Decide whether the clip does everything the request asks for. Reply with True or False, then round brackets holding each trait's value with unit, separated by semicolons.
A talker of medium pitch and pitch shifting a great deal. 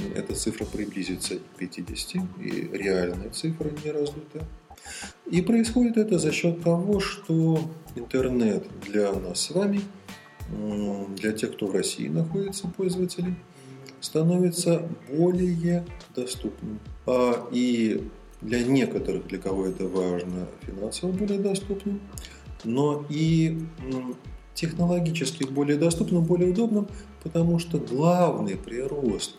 True (155 Hz; 7.7 semitones)